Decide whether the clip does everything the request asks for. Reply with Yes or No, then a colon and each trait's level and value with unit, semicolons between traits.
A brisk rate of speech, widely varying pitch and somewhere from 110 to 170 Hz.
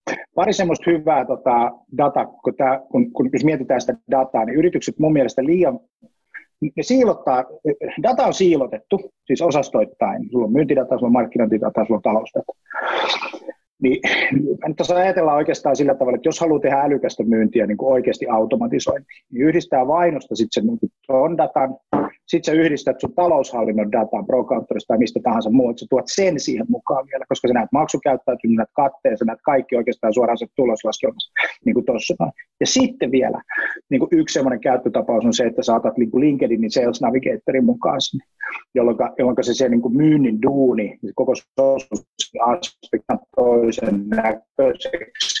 Yes: fast, 160 wpm; wide, 6.9 semitones; medium, 140 Hz